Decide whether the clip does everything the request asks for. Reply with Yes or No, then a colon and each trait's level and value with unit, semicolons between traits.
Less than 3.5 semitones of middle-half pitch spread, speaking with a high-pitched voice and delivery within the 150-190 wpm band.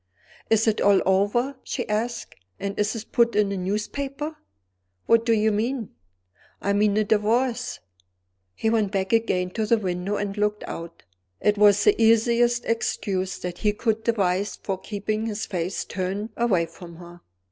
Yes: average, 2.8 semitones; high, 210 Hz; average, 165 wpm